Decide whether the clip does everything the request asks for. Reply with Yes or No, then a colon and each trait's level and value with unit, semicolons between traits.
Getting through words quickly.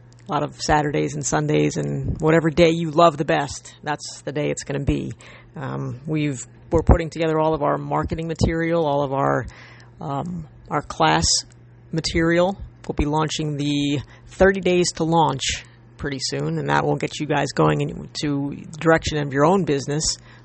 No: average, 180 wpm